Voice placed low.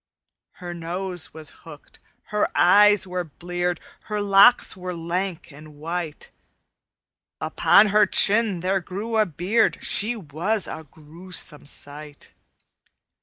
No: medium, 180 Hz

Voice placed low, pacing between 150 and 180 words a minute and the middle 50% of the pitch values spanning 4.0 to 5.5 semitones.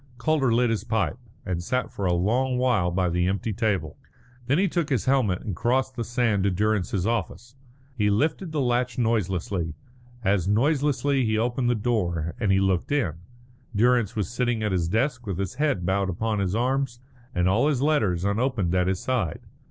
No: low, 110 Hz; average, 190 wpm; average, 5.0 semitones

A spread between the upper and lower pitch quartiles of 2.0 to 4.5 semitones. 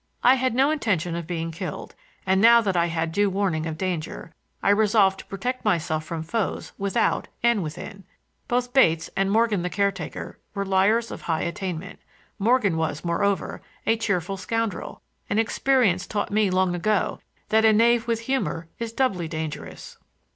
No: average, 4.9 semitones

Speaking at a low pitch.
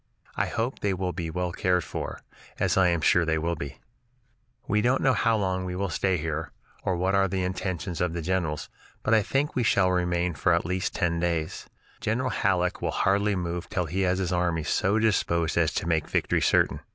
Yes: very low, 90 Hz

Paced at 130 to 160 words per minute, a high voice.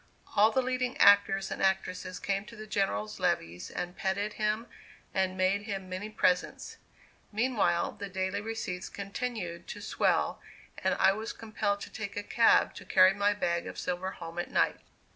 No: average, 170 wpm; high, 200 Hz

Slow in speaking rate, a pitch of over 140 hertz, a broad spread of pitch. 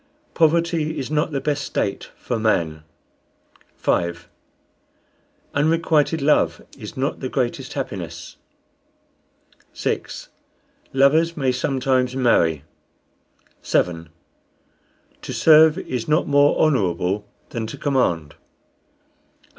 No: slow, 100 wpm; low, 135 Hz; wide, 6.0 semitones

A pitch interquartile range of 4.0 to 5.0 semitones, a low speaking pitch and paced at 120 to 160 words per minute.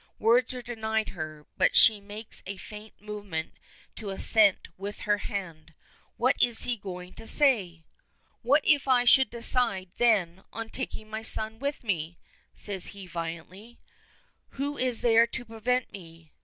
No: average, 4.3 semitones; high, 215 Hz; average, 155 wpm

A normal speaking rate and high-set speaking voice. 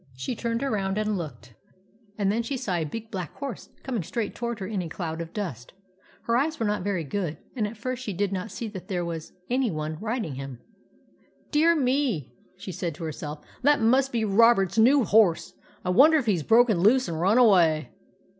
No: fast, 220 wpm; high, 205 Hz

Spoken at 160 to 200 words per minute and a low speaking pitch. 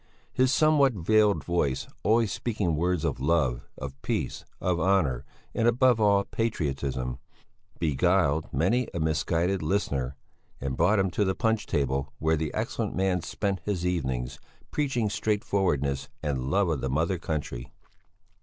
No: average, 145 wpm; very low, 85 Hz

